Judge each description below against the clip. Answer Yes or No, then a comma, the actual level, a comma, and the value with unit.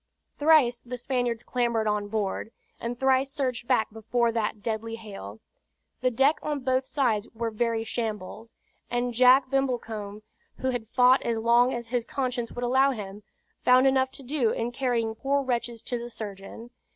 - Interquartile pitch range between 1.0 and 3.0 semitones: Yes, narrow, 2.6 semitones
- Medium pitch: No, high, 240 Hz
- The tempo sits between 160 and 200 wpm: Yes, average, 165 wpm